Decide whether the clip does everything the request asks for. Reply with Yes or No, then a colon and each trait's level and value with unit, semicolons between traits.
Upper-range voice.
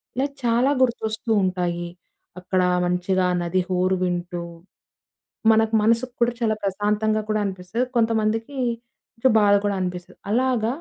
Yes: high, 215 Hz